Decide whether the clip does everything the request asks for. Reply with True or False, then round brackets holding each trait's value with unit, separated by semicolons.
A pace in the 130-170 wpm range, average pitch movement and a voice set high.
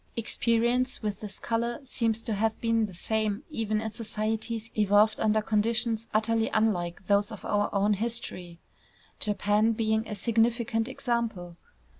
False (140 wpm; 1.6 semitones; 220 Hz)